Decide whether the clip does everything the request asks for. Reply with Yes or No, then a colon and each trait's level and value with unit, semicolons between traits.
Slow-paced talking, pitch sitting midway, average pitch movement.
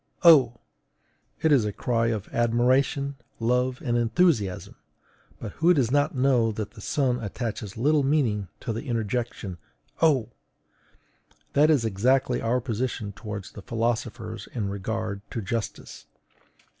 No: slow, 130 wpm; low, 120 Hz; average, 3.5 semitones